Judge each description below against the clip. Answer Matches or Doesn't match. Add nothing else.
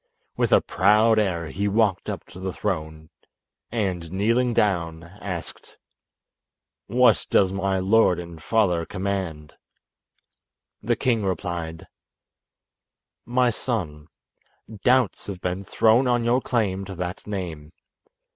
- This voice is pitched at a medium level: Doesn't match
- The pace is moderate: Doesn't match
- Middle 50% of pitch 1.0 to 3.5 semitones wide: Doesn't match